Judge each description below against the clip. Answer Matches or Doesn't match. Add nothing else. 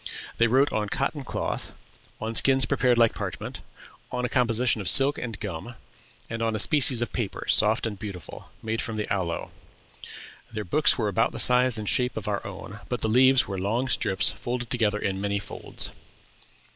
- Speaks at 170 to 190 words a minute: Matches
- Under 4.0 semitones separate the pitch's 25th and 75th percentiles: Matches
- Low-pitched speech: Matches